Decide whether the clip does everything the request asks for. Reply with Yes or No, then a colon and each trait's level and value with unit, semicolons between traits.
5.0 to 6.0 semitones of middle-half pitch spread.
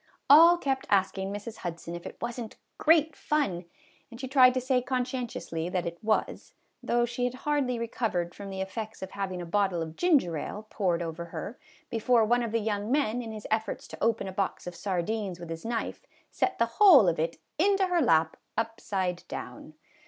Yes: wide, 5.6 semitones